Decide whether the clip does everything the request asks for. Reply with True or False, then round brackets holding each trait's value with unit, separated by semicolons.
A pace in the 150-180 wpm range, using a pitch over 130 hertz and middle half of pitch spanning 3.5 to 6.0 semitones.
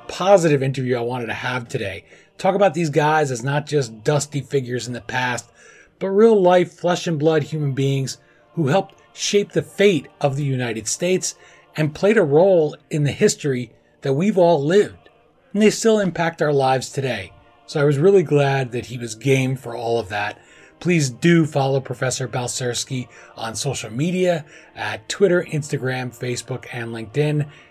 True (175 wpm; 140 Hz; 5.2 semitones)